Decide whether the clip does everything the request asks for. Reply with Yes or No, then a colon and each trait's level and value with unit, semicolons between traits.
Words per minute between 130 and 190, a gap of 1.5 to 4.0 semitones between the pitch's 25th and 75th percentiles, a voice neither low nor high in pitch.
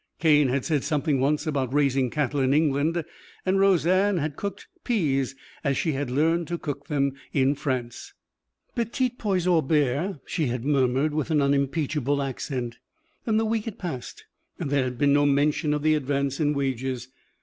Yes: average, 175 wpm; average, 3.1 semitones; medium, 145 Hz